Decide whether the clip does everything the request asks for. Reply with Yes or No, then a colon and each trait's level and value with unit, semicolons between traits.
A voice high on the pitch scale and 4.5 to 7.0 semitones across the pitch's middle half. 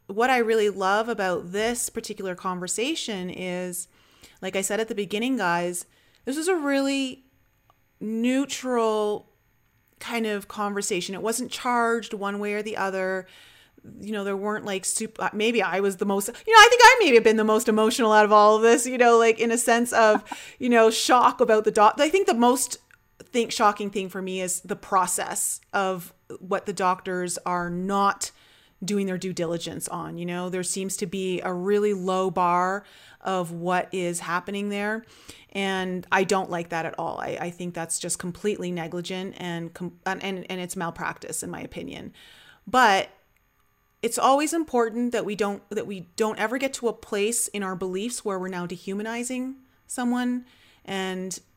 No: high, 205 Hz; average, 3.7 semitones